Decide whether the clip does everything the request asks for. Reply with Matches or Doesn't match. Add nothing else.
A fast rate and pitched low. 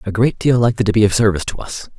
Matches